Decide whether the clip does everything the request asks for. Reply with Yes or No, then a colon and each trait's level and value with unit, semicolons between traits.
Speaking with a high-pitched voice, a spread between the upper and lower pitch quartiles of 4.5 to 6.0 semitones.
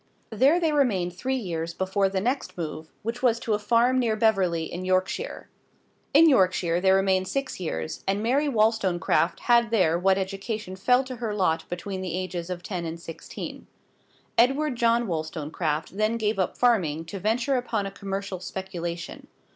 Yes: high, 195 Hz; average, 4.9 semitones